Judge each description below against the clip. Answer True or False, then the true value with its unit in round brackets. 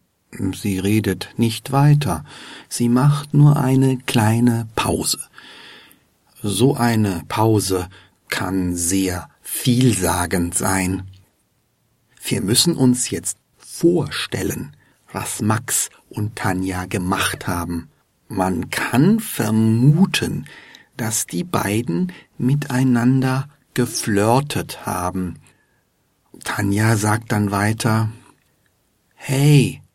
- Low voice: True (110 Hz)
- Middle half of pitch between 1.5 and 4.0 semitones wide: False (5.0 semitones)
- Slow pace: True (85 wpm)